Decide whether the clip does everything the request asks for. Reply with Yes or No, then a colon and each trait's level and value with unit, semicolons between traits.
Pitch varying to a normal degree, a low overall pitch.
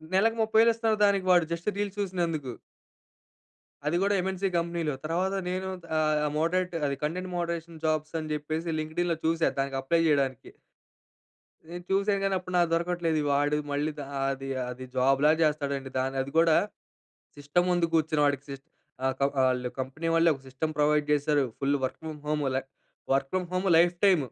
No: average, 3.7 semitones; medium, 160 Hz